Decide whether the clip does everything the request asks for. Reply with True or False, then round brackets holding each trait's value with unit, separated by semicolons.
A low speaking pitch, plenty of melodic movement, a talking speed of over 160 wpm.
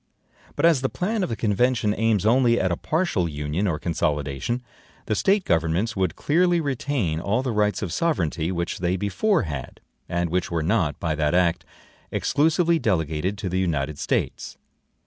True (95 Hz; 7.6 semitones; 170 wpm)